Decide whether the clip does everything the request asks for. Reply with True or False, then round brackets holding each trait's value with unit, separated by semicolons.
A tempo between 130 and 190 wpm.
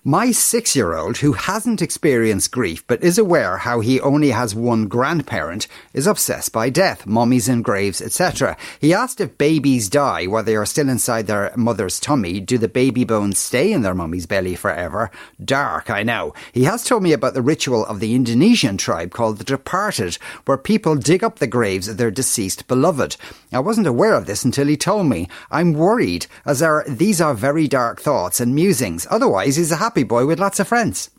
False (200 wpm)